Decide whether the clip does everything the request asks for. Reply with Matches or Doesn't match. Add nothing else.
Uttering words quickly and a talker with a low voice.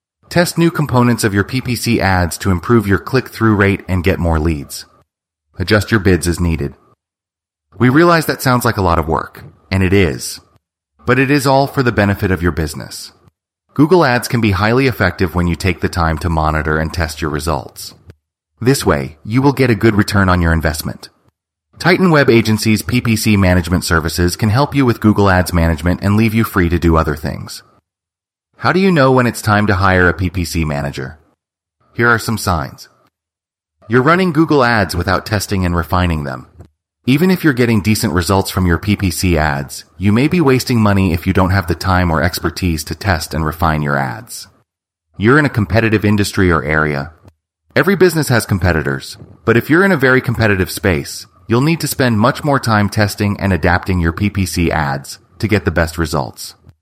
Doesn't match